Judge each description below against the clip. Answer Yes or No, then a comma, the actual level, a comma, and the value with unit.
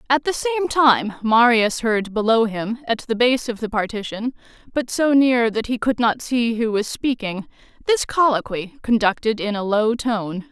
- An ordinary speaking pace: Yes, average, 185 wpm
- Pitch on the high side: Yes, high, 235 Hz